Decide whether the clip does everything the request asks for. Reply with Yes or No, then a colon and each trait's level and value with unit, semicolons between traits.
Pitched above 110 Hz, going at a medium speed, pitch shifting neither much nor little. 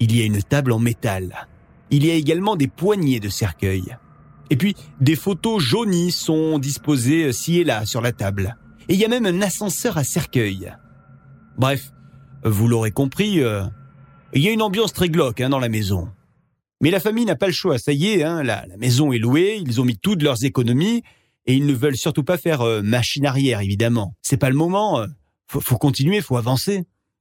No: low, 135 Hz; average, 210 wpm; wide, 6.1 semitones